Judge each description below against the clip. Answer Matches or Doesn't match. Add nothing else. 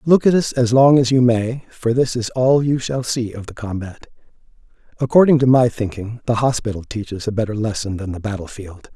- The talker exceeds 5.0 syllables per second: Matches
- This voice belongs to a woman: Doesn't match